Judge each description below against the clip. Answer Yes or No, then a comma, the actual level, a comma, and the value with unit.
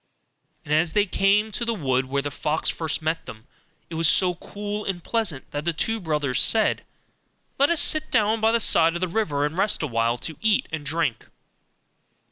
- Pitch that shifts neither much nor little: No, wide, 6.2 semitones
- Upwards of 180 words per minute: Yes, fast, 205 wpm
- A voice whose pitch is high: No, medium, 170 Hz